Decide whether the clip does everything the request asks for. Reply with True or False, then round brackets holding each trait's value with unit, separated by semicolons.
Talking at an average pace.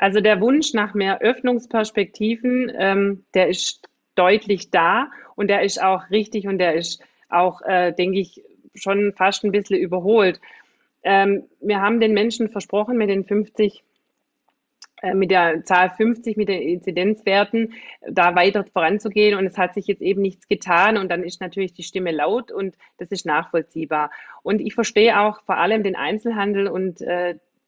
True (165 wpm)